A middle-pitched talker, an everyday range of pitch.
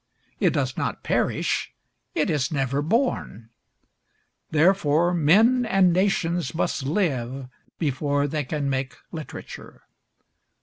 Yes: medium, 155 Hz; average, 4.6 semitones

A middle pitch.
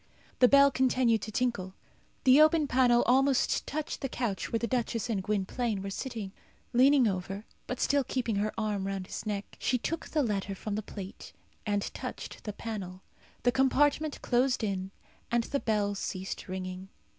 No: high, 225 Hz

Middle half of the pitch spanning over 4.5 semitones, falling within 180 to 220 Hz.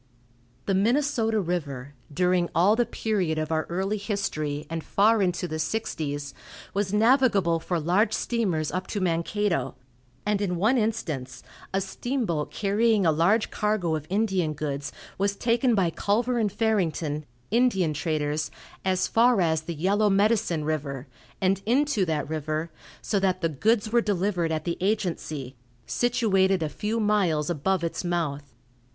Yes: average, 5.1 semitones; medium, 185 Hz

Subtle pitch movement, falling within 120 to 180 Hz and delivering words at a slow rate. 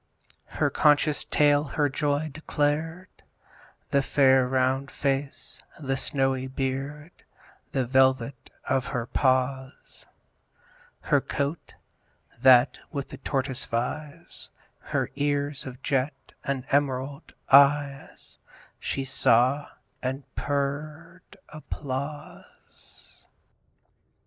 Yes: narrow, 1.8 semitones; medium, 140 Hz; slow, 90 wpm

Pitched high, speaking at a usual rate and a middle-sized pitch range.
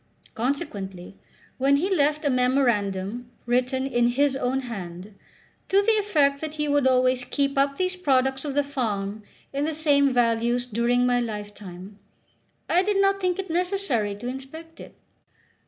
Yes: very high, 265 Hz; average, 155 wpm; average, 4.2 semitones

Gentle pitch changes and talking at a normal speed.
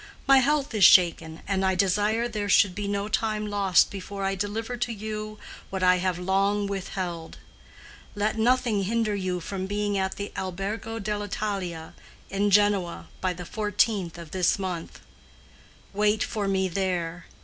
Yes: narrow, 2.3 semitones; average, 160 wpm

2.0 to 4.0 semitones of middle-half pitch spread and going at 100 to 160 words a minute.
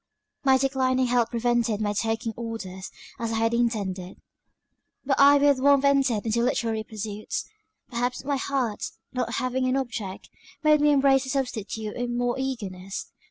Yes: average, 3.2 semitones; average, 155 wpm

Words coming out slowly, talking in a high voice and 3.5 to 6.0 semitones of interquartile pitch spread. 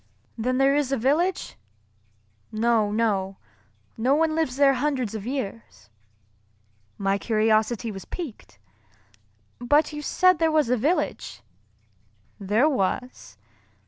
Yes: slow, 115 wpm; very high, 250 Hz; average, 5.3 semitones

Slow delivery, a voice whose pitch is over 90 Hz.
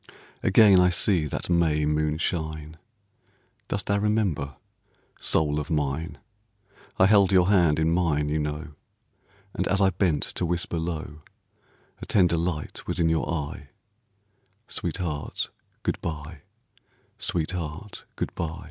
No: slow, 130 wpm; very low, 80 Hz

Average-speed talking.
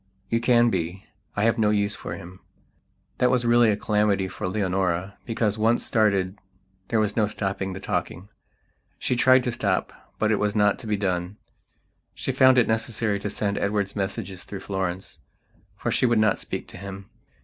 Yes: average, 180 wpm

